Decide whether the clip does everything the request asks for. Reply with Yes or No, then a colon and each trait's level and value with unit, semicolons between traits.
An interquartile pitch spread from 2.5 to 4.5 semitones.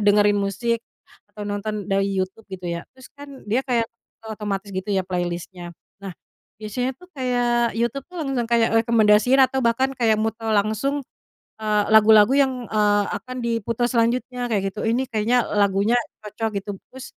Yes: average, 3.2 semitones